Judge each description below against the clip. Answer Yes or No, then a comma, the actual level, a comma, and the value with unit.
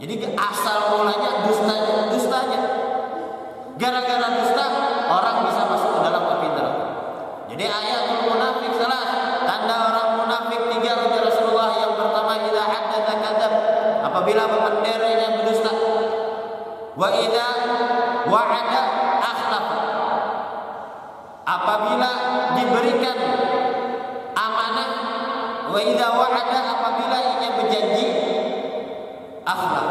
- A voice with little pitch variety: Yes, narrow, 1.8 semitones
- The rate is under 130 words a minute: Yes, average, 90 wpm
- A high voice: Yes, high, 225 Hz